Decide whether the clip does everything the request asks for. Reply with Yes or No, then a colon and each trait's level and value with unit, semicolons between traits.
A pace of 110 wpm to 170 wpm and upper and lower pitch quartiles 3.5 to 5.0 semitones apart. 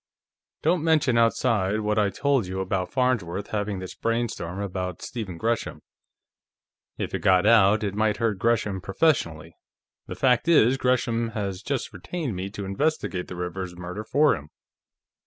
Yes: average, 155 wpm; average, 4.4 semitones